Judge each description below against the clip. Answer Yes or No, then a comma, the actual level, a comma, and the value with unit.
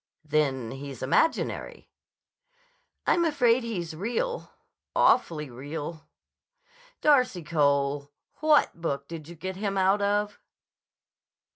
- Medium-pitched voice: Yes, medium, 170 Hz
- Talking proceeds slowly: Yes, slow, 100 wpm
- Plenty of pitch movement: Yes, wide, 7.7 semitones